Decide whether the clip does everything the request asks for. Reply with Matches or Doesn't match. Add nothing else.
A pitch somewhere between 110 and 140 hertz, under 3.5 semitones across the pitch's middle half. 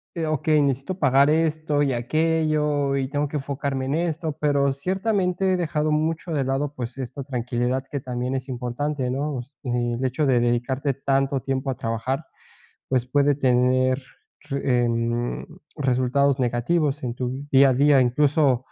Matches